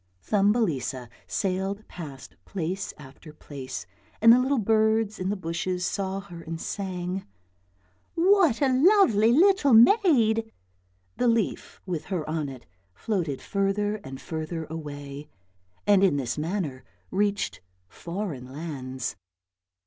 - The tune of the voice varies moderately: No, wide, 6.4 semitones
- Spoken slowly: Yes, slow, 125 wpm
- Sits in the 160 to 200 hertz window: Yes, high, 190 Hz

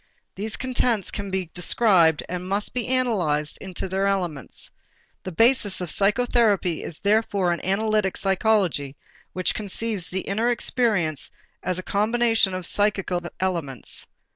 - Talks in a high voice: Yes, high, 195 Hz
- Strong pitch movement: No, average, 3.5 semitones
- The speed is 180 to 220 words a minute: No, slow, 135 wpm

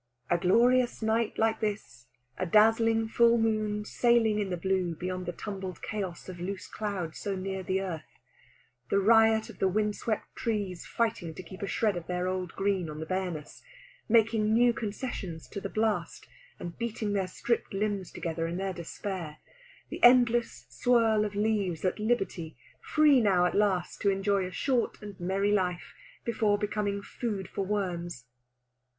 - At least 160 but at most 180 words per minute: Yes, average, 170 wpm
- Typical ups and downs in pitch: Yes, average, 3.3 semitones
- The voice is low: No, high, 200 Hz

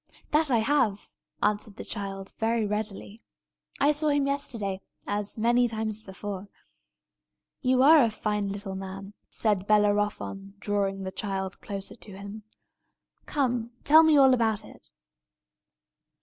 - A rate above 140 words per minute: No, slow, 135 wpm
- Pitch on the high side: Yes, high, 210 Hz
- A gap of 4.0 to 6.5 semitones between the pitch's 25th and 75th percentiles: No, average, 3.5 semitones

